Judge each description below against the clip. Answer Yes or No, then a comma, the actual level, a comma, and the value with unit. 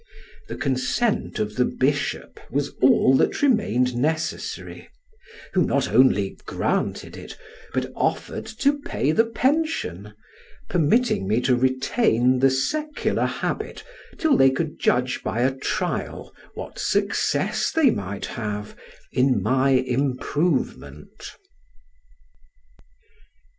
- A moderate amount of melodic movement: No, wide, 7.0 semitones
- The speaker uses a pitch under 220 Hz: Yes, low, 135 Hz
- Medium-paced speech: No, slow, 110 wpm